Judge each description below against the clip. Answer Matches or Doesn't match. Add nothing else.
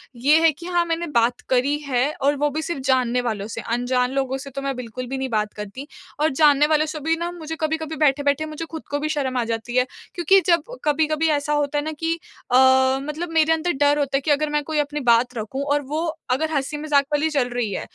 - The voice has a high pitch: Matches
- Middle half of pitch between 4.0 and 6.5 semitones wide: Doesn't match